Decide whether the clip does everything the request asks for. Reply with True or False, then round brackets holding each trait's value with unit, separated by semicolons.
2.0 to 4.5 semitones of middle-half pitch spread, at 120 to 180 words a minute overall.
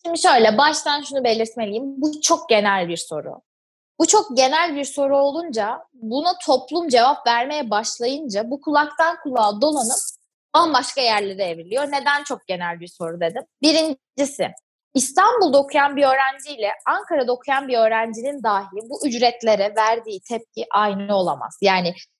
False (5.2 semitones; 140 wpm)